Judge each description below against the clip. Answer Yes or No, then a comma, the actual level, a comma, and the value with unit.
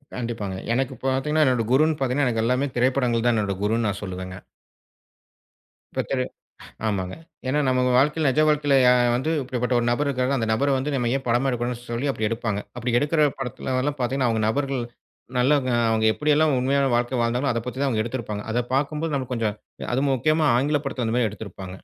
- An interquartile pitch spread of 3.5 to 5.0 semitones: No, average, 3.1 semitones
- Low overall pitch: Yes, low, 125 Hz